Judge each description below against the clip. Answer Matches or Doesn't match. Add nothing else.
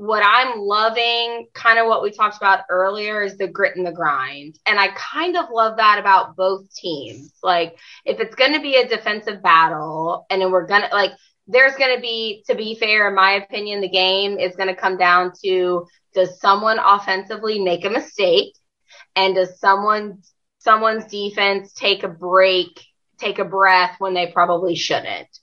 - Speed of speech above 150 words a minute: Matches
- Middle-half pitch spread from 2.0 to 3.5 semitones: Matches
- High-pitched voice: Matches